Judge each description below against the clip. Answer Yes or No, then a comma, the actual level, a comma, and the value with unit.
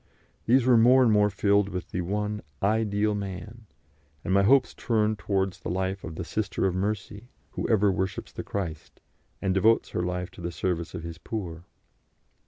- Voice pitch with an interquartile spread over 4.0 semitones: No, average, 2.8 semitones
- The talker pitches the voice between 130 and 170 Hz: No, low, 100 Hz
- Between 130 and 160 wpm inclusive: No, average, 185 wpm